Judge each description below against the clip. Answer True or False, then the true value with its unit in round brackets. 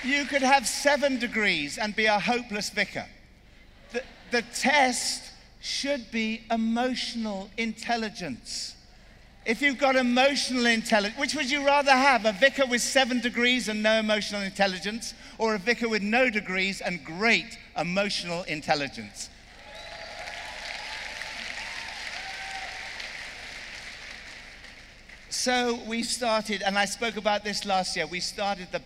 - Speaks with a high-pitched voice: True (225 Hz)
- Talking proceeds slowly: True (125 wpm)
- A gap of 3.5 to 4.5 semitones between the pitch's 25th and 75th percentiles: True (3.9 semitones)